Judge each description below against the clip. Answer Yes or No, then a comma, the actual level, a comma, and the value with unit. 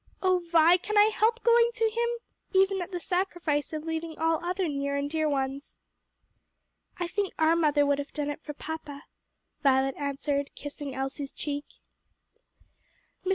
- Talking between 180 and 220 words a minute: No, average, 160 wpm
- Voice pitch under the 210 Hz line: No, very high, 315 Hz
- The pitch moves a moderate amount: Yes, average, 4.3 semitones